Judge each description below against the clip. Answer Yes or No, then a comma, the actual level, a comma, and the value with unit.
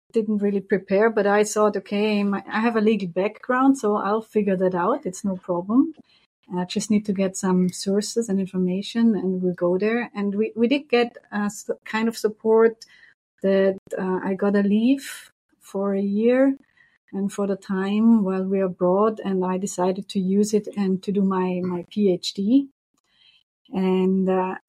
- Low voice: No, high, 205 Hz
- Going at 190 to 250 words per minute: No, average, 180 wpm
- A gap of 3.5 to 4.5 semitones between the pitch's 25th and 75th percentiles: No, average, 2.7 semitones